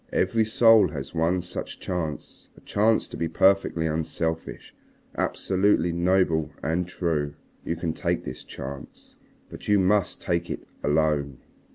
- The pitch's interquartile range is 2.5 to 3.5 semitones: Yes, average, 3.1 semitones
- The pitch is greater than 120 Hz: No, very low, 85 Hz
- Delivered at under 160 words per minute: Yes, average, 140 wpm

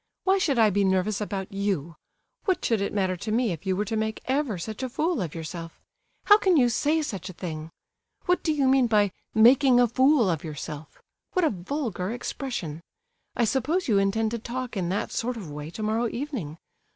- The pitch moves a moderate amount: No, wide, 5.8 semitones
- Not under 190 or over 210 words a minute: Yes, fast, 205 wpm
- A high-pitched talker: Yes, high, 220 Hz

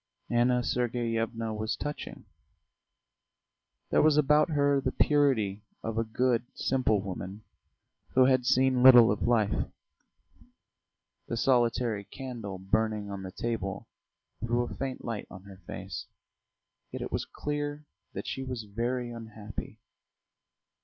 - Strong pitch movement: No, average, 3.2 semitones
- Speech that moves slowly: Yes, slow, 125 wpm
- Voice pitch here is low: Yes, low, 120 Hz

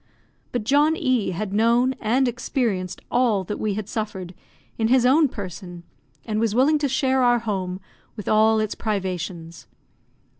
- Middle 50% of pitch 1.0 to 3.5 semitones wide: No, average, 4.6 semitones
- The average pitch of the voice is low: No, high, 220 Hz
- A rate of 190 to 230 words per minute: No, average, 155 wpm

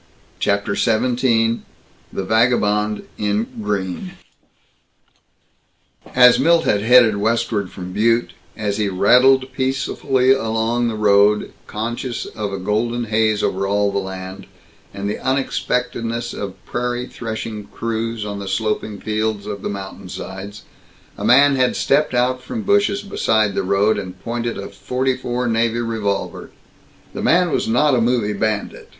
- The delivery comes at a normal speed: No, slow, 130 wpm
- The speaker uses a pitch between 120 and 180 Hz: No, low, 110 Hz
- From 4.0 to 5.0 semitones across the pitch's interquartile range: No, average, 3.4 semitones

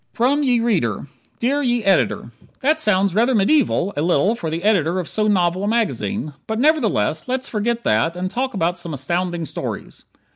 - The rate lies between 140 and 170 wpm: No, average, 180 wpm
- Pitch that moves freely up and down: Yes, wide, 5.7 semitones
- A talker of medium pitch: No, high, 205 Hz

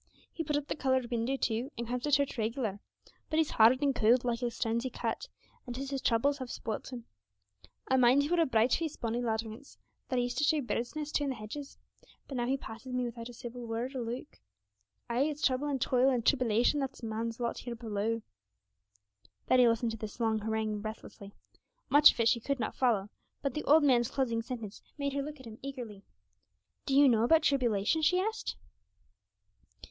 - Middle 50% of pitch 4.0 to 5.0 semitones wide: No, average, 3.4 semitones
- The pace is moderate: No, fast, 215 wpm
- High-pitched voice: Yes, high, 245 Hz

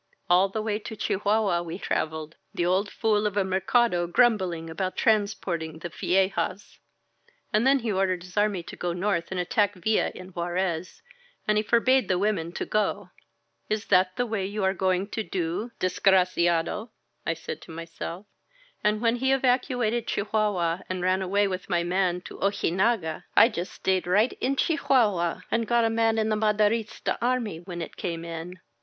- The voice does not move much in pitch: No, average, 3.6 semitones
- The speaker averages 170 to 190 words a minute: Yes, average, 180 wpm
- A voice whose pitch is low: No, high, 195 Hz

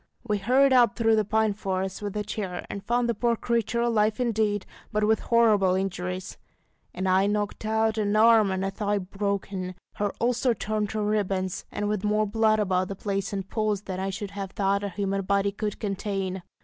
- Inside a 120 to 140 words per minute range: No, average, 200 wpm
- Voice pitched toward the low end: No, high, 205 Hz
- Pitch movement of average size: No, narrow, 2.0 semitones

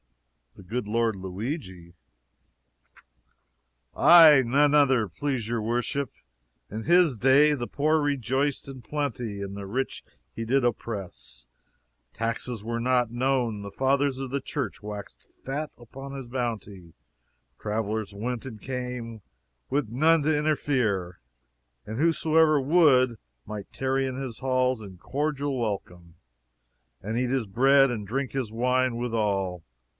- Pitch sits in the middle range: No, low, 125 Hz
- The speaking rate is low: Yes, slow, 130 wpm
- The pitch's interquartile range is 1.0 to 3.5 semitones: No, average, 4.1 semitones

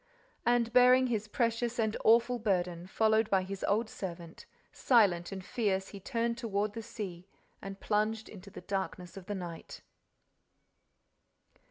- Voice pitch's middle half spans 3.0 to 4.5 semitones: Yes, average, 3.4 semitones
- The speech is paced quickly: No, average, 145 wpm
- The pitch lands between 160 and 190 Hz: No, high, 210 Hz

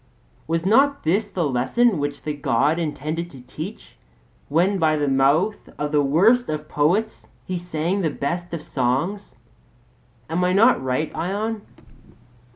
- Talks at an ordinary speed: Yes, average, 150 wpm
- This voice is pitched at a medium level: Yes, medium, 165 Hz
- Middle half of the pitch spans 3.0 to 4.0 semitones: No, average, 5.0 semitones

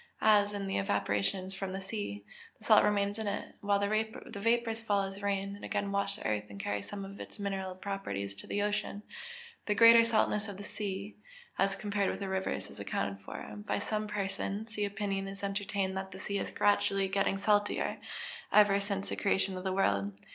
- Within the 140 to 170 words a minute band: No, average, 200 wpm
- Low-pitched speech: No, high, 200 Hz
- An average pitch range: No, narrow, 1.2 semitones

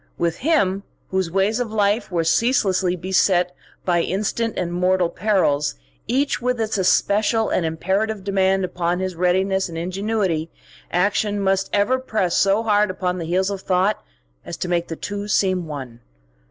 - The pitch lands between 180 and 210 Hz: Yes, high, 190 Hz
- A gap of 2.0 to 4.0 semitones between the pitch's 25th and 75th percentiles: Yes, average, 2.7 semitones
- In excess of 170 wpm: No, average, 160 wpm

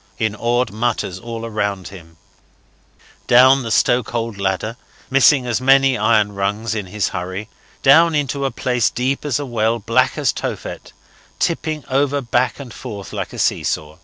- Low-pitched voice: Yes, low, 115 Hz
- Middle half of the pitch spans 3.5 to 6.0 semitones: Yes, average, 4.3 semitones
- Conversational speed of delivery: Yes, average, 160 wpm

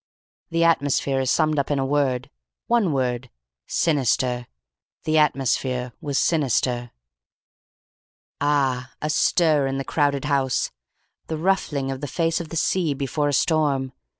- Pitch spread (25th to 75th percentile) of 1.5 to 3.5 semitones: Yes, average, 2.8 semitones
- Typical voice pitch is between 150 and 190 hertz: No, medium, 140 Hz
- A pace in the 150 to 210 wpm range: No, average, 140 wpm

